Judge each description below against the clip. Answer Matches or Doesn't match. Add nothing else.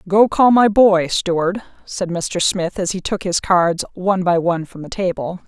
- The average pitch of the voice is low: Doesn't match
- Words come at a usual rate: Doesn't match